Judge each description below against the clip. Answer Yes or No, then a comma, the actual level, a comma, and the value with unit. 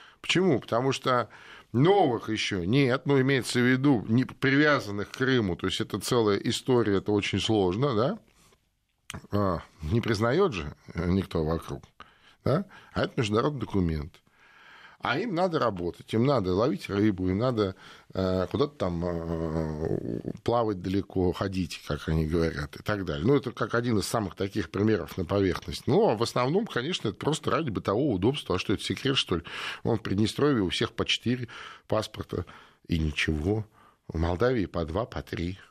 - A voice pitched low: Yes, low, 100 Hz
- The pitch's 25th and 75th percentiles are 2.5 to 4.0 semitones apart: No, average, 5.1 semitones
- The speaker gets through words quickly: Yes, fast, 165 wpm